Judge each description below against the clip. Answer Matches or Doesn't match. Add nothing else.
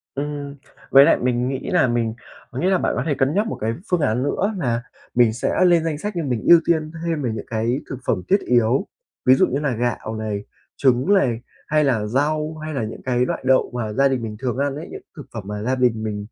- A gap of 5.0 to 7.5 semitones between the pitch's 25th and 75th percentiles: Doesn't match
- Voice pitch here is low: Matches